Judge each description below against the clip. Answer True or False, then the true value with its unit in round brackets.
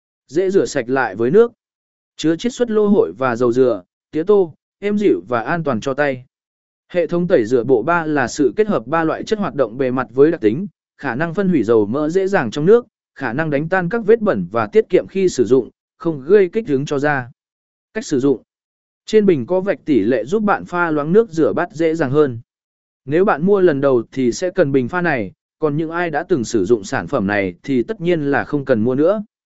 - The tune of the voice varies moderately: False (6.4 semitones)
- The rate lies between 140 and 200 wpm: False (245 wpm)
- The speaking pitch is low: False (175 Hz)